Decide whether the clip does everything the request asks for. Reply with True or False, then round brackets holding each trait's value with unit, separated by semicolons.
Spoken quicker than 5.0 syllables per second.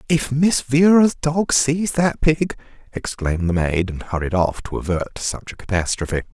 False (4.6 syllables/s)